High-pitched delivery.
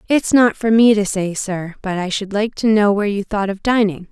Yes: high, 205 Hz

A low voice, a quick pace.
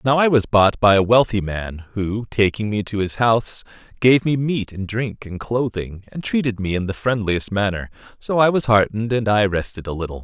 Yes: low, 110 Hz; fast, 215 wpm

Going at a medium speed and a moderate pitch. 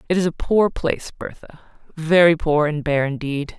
Yes: average, 185 wpm; medium, 160 Hz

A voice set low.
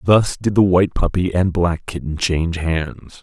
Yes: very low, 90 Hz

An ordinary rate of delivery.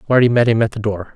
No: fast, 310 wpm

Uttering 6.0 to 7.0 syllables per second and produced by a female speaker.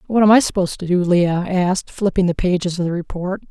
Yes: 6.1 syllables/s; female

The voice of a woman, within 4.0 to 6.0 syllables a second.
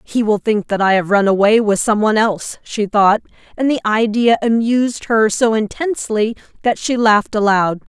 Yes: female; 5.1 syllables/s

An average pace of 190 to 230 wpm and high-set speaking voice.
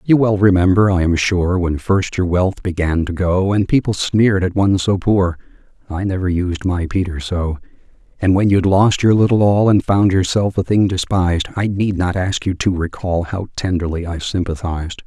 No: average, 200 wpm; very low, 95 Hz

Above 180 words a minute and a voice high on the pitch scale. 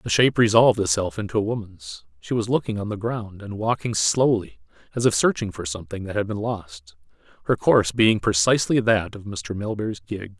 No: average, 195 wpm; low, 105 Hz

